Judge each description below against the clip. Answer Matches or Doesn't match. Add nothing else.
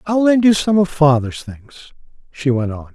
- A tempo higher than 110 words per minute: Matches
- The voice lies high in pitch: Doesn't match